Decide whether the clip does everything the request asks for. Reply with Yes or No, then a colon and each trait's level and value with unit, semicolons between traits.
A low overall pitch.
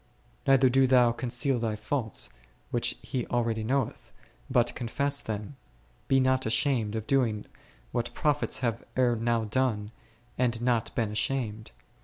Yes: low, 120 Hz